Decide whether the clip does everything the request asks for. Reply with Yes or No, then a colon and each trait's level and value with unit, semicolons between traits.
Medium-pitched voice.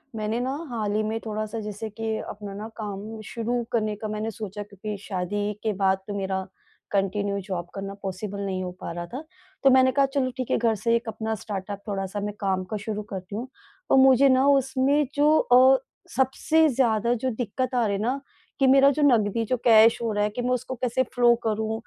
No: high, 220 Hz